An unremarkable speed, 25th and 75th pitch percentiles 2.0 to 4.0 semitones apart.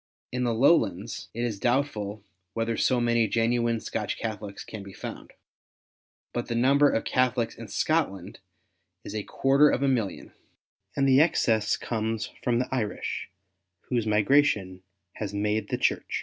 Yes: average, 150 wpm; average, 3.2 semitones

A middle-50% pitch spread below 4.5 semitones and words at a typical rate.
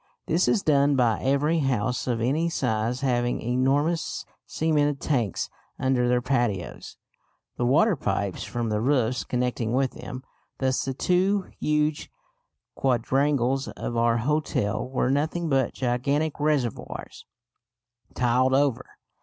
No: average, 3.3 semitones; slow, 125 wpm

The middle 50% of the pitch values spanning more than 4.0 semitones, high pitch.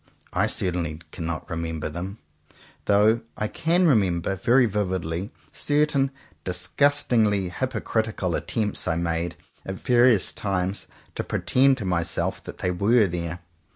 No: average, 5.1 semitones; very low, 95 Hz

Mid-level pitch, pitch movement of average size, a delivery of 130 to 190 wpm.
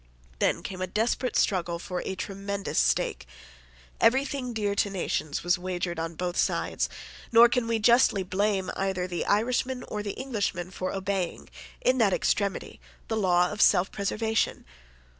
No: high, 195 Hz; average, 3.6 semitones; average, 155 wpm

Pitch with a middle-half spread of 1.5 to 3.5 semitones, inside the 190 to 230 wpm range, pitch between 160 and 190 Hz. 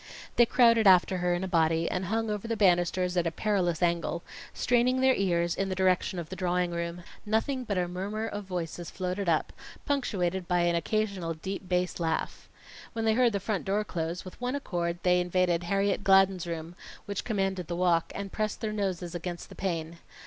Yes: average, 3.0 semitones; average, 200 wpm; medium, 185 Hz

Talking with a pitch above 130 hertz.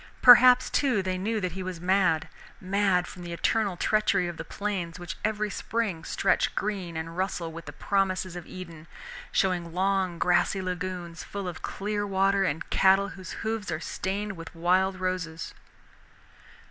Yes: medium, 185 Hz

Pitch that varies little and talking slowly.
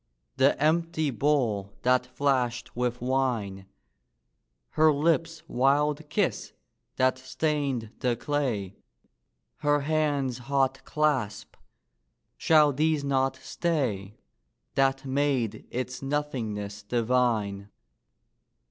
No: average, 3.6 semitones; slow, 90 wpm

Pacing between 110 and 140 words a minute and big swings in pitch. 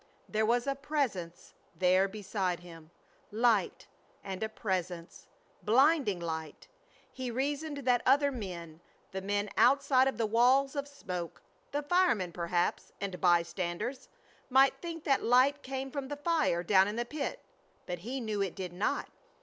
No: average, 155 wpm; wide, 6.9 semitones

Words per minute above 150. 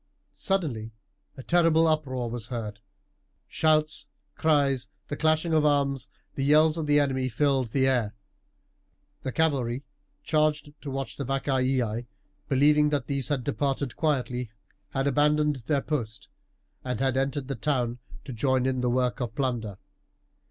No: average, 145 wpm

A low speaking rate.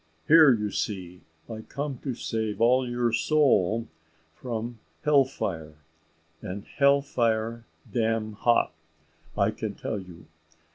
Yes: slow, 125 wpm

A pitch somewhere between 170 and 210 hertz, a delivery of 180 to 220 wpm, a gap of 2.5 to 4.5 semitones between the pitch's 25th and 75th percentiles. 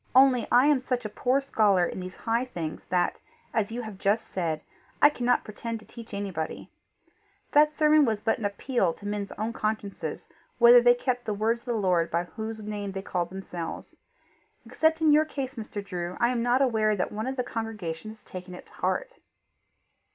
No: high, 220 Hz; average, 200 wpm; average, 4.1 semitones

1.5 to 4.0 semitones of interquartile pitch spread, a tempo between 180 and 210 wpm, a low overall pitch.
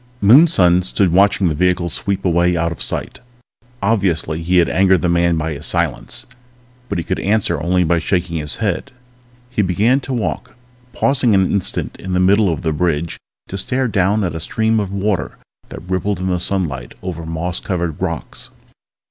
Yes: average, 2.9 semitones; average, 185 wpm; very low, 90 Hz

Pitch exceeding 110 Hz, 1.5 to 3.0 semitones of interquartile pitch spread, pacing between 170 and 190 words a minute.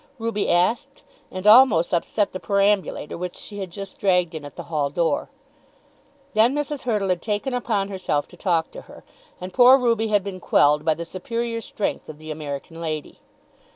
No: high, 190 Hz; average, 4.9 semitones; average, 185 wpm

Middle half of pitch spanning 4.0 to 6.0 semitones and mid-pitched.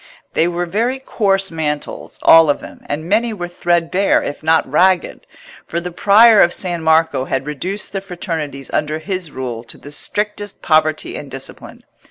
Yes: average, 4.3 semitones; medium, 170 Hz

